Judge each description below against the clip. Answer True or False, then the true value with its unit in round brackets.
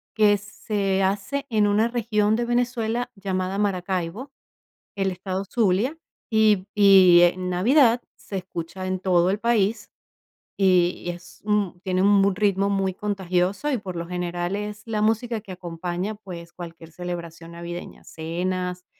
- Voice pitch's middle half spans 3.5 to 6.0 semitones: False (2.9 semitones)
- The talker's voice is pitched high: True (195 Hz)